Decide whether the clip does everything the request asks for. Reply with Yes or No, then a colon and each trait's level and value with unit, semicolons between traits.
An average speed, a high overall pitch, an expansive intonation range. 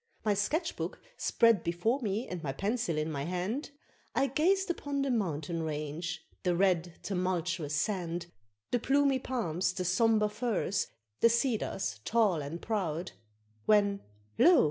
Yes: average, 145 wpm; high, 195 Hz; wide, 5.7 semitones